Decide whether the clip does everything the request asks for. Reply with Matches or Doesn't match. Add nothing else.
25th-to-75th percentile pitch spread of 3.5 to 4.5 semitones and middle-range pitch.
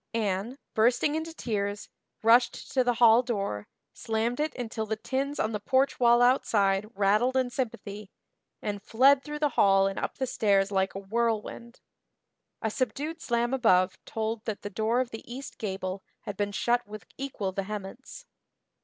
Doesn't match